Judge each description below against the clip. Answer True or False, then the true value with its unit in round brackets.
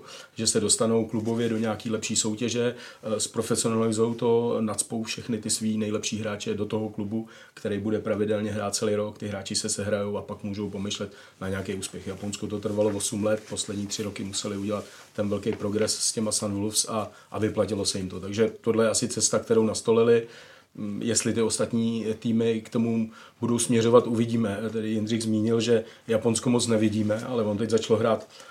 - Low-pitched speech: True (110 Hz)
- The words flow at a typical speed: False (185 wpm)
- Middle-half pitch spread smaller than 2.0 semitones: True (1.5 semitones)